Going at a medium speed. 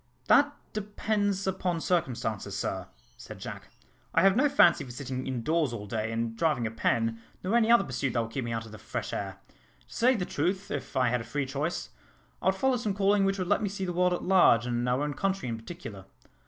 No: fast, 230 wpm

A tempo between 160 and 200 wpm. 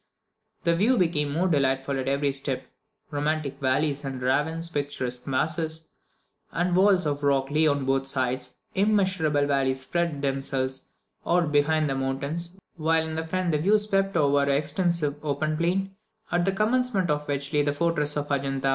Yes: average, 165 wpm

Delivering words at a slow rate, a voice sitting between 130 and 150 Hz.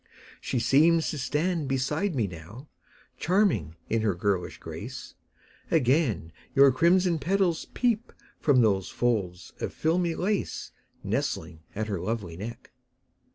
Yes: slow, 125 wpm; low, 135 Hz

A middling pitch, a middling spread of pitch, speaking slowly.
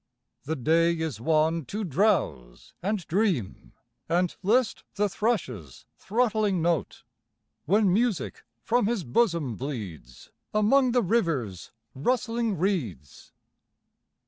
No: medium, 175 Hz; wide, 8.4 semitones; slow, 105 wpm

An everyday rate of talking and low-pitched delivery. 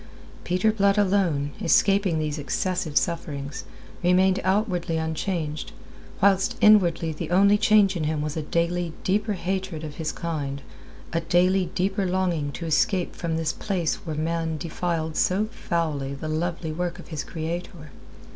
No: average, 145 wpm; medium, 170 Hz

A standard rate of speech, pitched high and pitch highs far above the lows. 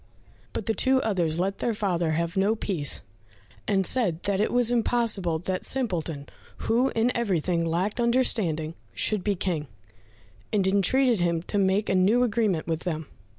No: average, 160 wpm; high, 195 Hz; average, 5.0 semitones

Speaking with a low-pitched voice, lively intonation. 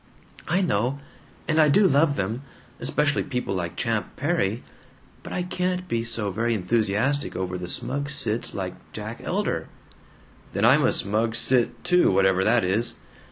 Yes: low, 115 Hz; wide, 6.3 semitones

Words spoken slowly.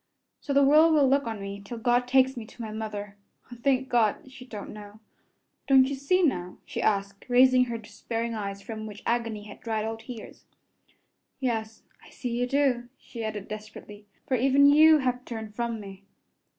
No: average, 190 wpm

